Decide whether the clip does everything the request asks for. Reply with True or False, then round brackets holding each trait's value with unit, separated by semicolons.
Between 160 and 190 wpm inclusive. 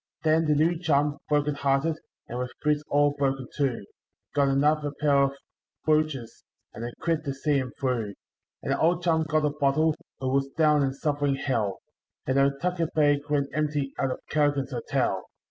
True (180 wpm)